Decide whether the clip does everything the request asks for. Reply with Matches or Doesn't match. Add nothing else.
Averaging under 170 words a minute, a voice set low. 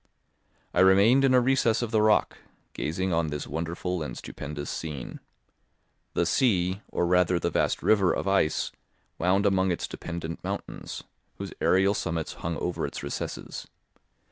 Matches